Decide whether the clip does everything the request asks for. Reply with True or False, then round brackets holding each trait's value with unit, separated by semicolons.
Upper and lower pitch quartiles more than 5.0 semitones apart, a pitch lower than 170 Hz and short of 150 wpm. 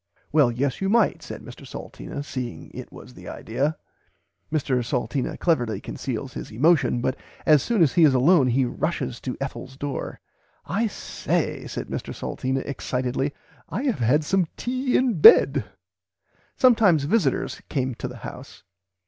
False (5.6 semitones; 140 Hz; 155 wpm)